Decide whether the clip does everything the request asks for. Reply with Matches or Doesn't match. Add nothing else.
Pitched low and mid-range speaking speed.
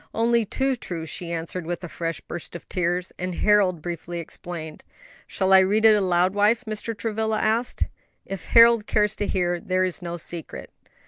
Doesn't match